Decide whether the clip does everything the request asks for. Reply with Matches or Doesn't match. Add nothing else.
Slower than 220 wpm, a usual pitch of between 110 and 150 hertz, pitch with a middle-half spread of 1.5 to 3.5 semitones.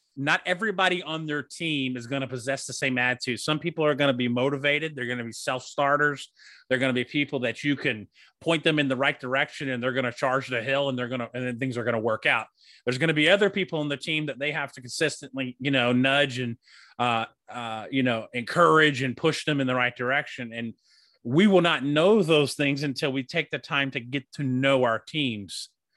Doesn't match